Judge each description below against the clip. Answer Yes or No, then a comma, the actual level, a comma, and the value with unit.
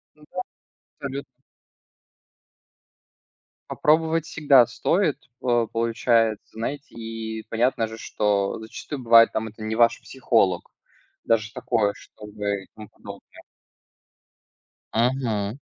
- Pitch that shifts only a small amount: No, average, 3.2 semitones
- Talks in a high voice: No, low, 115 Hz